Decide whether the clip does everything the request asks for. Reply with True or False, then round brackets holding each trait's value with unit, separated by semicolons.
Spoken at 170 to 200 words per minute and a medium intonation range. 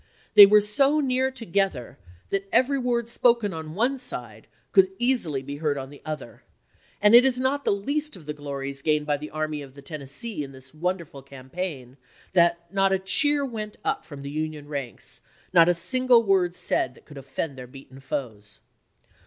False (185 wpm; 8.4 semitones)